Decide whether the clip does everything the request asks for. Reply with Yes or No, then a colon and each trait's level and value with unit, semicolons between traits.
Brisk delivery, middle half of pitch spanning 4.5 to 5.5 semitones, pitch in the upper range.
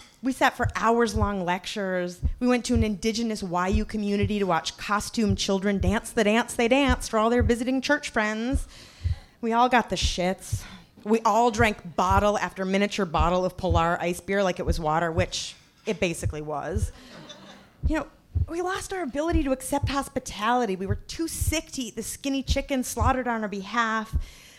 No: average, 180 wpm; average, 4.8 semitones; high, 220 Hz